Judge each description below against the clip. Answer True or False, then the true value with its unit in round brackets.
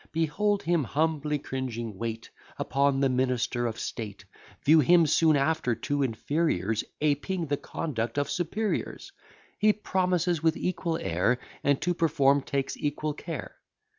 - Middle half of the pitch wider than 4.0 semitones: True (4.4 semitones)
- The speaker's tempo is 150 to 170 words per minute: False (135 wpm)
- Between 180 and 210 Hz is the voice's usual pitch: False (145 Hz)